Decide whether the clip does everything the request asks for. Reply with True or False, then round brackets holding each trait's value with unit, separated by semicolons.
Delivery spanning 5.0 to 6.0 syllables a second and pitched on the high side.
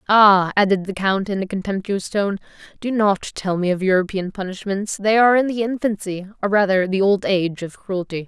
True (5.4 syllables/s; 195 Hz)